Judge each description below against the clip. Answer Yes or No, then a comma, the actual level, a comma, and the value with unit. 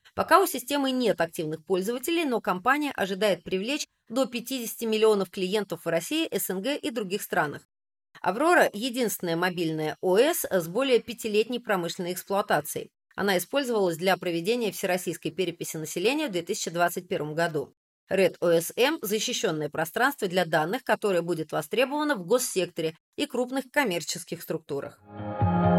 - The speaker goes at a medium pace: Yes, average, 125 wpm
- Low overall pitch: No, high, 190 Hz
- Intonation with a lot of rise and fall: Yes, wide, 5.8 semitones